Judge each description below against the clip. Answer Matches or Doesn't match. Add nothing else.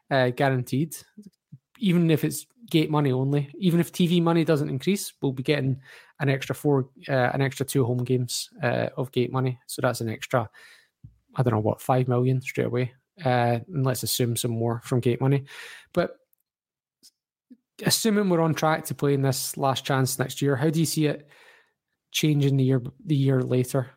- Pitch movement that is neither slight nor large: Matches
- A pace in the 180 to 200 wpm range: Matches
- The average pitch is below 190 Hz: Matches